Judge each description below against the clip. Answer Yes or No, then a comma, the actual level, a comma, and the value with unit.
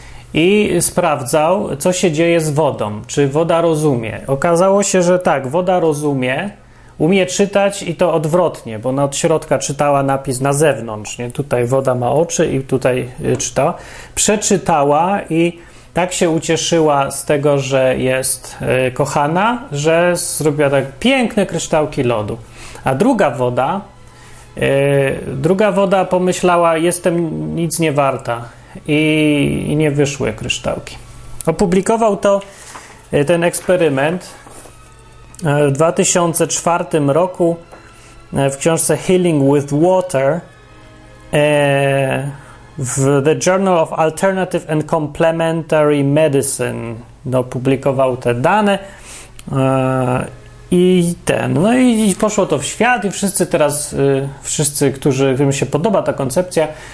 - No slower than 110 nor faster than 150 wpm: Yes, average, 115 wpm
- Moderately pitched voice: Yes, medium, 155 Hz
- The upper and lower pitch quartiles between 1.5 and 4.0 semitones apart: No, average, 4.7 semitones